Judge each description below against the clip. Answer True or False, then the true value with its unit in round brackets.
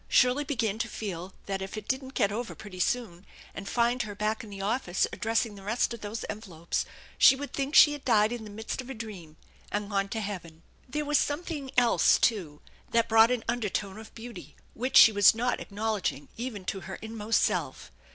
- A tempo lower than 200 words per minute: False (205 wpm)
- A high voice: True (220 Hz)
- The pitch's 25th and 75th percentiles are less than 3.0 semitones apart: False (3.5 semitones)